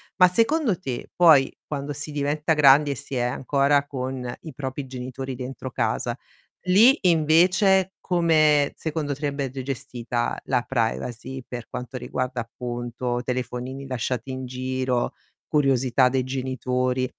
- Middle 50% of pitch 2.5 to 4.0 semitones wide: Yes, average, 2.8 semitones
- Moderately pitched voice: No, low, 130 Hz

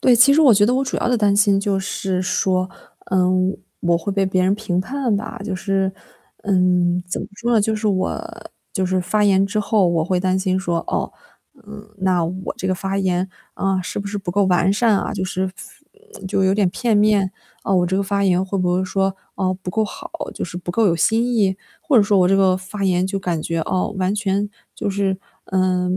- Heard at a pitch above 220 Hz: No, high, 190 Hz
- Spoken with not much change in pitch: Yes, narrow, 1.9 semitones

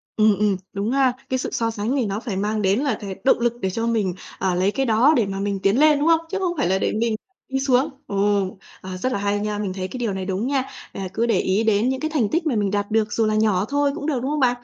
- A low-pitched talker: No, high, 220 Hz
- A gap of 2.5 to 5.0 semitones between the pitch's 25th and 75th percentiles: Yes, average, 4.5 semitones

